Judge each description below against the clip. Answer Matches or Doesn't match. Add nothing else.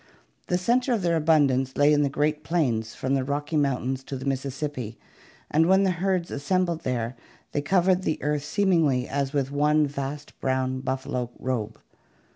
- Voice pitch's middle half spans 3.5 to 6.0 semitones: Matches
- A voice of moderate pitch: Matches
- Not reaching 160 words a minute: Doesn't match